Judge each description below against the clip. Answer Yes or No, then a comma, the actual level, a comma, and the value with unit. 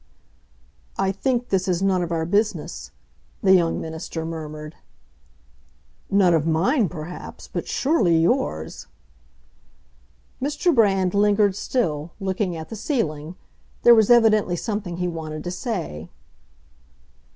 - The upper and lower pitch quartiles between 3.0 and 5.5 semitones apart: Yes, average, 4.7 semitones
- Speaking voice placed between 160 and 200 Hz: Yes, medium, 185 Hz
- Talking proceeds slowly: Yes, slow, 120 wpm